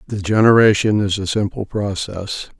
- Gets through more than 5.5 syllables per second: No, 4.8 syllables/s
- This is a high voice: No, low, 100 Hz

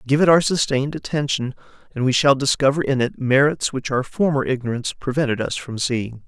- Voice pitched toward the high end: No, low, 135 Hz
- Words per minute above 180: Yes, average, 190 wpm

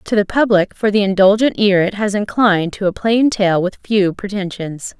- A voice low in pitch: No, high, 200 Hz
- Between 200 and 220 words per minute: Yes, fast, 205 wpm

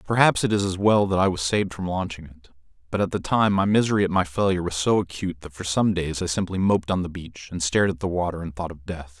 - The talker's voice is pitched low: Yes, very low, 90 Hz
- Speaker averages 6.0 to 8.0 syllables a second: Yes, 6.5 syllables/s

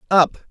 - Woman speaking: No, male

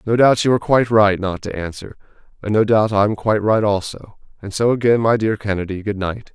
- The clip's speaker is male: Yes, male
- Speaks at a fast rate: Yes, fast, 225 wpm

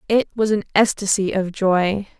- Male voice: No, female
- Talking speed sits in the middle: Yes, average, 165 wpm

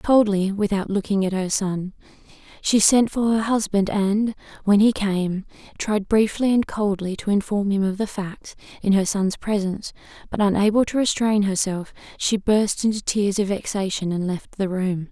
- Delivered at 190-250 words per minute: No, average, 175 wpm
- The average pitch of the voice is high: Yes, high, 200 Hz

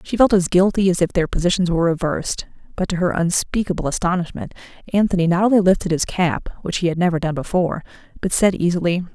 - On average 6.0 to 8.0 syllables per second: Yes, 6.5 syllables/s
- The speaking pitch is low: No, medium, 180 Hz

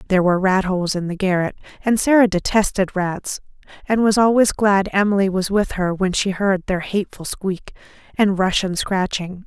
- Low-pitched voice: No, high, 195 Hz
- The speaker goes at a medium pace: Yes, average, 185 wpm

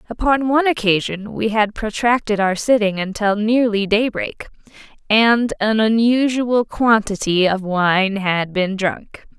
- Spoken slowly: Yes, slow, 130 wpm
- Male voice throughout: No, female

